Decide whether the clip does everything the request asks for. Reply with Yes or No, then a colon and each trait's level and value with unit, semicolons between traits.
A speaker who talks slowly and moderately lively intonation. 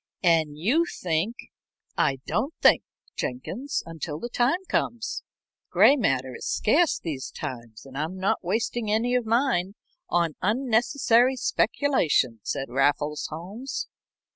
No: slow, 130 wpm; wide, 8.5 semitones